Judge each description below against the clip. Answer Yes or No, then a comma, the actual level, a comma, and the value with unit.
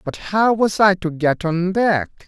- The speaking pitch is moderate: Yes, medium, 180 Hz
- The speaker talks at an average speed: No, fast, 210 wpm